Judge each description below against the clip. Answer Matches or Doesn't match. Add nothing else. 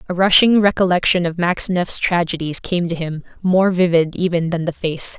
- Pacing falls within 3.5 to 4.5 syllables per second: Doesn't match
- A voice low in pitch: Doesn't match